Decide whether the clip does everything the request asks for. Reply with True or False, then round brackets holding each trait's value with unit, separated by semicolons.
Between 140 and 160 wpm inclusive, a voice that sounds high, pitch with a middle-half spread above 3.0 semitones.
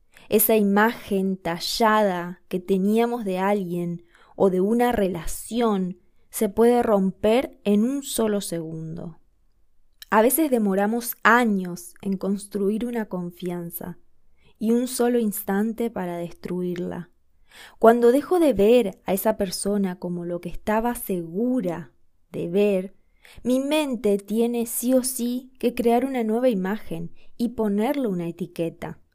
False (125 wpm; 205 Hz; 4.7 semitones)